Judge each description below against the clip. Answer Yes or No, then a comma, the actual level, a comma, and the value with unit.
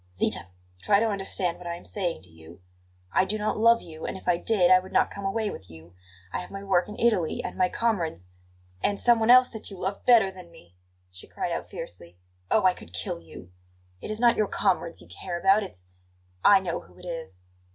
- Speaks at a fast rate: Yes, fast, 230 wpm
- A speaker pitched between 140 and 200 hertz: Yes, medium, 185 Hz